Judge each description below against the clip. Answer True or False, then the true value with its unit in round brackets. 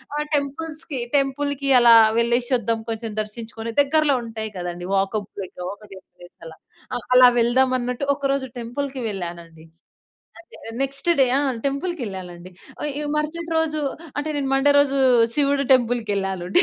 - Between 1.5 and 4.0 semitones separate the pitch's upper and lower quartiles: False (5.1 semitones)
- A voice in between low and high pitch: False (245 Hz)